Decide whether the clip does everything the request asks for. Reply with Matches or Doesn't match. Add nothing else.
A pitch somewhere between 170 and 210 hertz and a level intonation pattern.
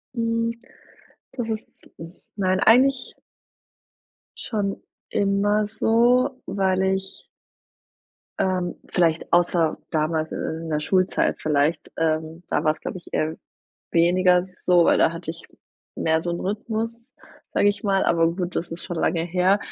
Doesn't match